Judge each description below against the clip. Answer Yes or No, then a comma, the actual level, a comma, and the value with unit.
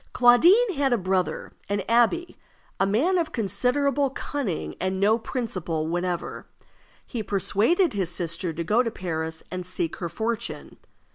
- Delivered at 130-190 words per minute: Yes, average, 145 wpm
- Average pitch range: No, wide, 6.0 semitones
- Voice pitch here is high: Yes, high, 210 Hz